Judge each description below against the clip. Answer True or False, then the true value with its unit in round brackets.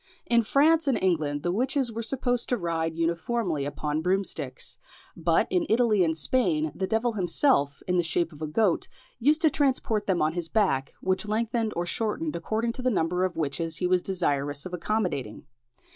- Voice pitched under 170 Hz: False (185 Hz)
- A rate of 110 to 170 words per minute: False (185 wpm)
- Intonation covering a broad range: True (6.1 semitones)